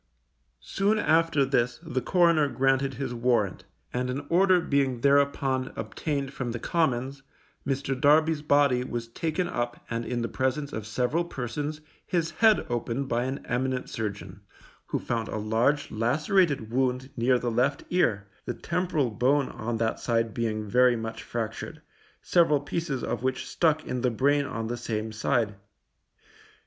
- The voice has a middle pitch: No, low, 130 Hz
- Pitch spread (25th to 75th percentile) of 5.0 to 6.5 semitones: No, average, 3.7 semitones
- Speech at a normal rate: Yes, average, 155 wpm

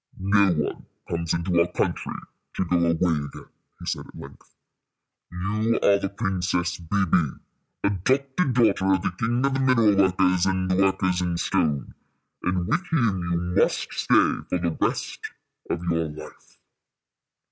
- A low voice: Yes, very low, 95 Hz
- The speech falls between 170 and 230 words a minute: No, average, 155 wpm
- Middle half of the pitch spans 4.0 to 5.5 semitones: No, average, 2.8 semitones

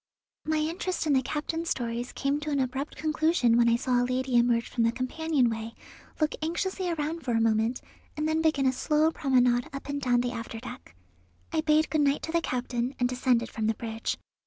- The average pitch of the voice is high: Yes, very high, 260 Hz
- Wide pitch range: No, average, 4.5 semitones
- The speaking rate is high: Yes, fast, 210 wpm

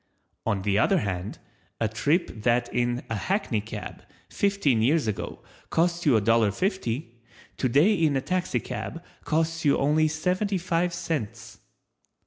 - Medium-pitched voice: Yes, medium, 145 Hz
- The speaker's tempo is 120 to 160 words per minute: Yes, average, 140 wpm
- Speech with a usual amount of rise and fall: No, wide, 7.1 semitones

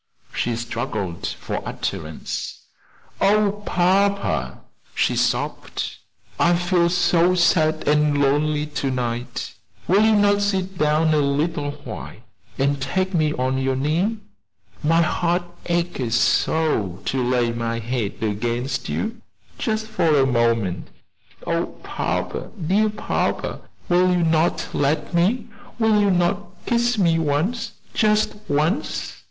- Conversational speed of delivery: No, slow, 125 wpm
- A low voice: No, medium, 160 Hz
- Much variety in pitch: Yes, wide, 6.1 semitones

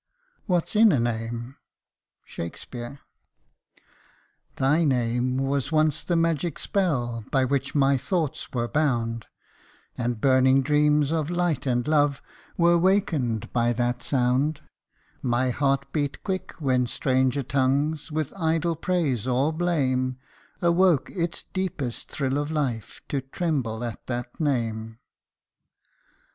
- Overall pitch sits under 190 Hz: Yes, medium, 140 Hz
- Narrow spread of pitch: No, average, 4.3 semitones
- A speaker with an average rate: No, slow, 125 wpm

